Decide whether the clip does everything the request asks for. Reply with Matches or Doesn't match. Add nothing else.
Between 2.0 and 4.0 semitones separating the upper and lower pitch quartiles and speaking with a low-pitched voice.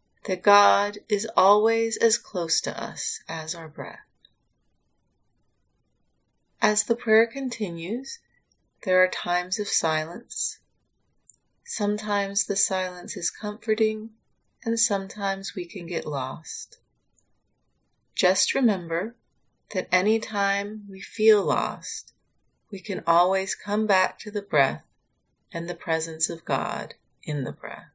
Doesn't match